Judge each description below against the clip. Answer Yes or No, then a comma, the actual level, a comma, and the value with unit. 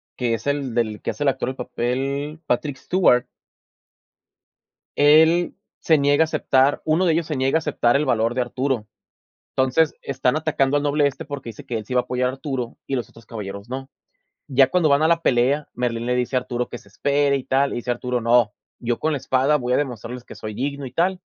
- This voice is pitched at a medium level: No, low, 130 Hz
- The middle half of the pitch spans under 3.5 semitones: Yes, average, 3.0 semitones